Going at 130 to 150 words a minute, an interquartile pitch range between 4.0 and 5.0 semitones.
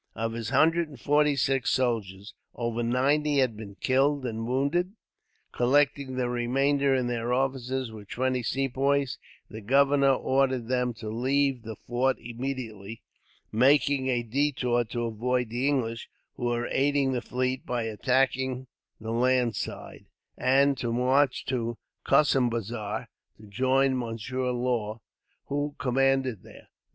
No: slow, 135 wpm; narrow, 2.6 semitones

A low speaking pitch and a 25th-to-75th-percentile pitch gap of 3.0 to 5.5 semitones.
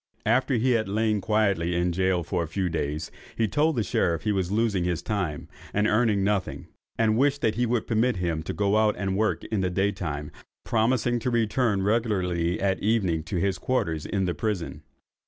Yes: low, 100 Hz; average, 4.1 semitones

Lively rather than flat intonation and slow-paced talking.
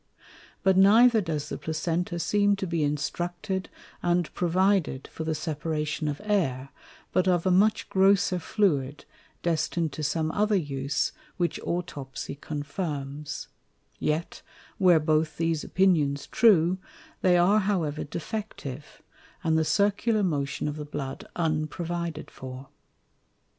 No: average, 4.0 semitones; slow, 125 wpm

